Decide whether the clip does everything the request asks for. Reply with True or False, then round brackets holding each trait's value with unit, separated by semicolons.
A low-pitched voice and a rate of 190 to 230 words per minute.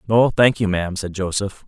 True (100 Hz; 215 wpm)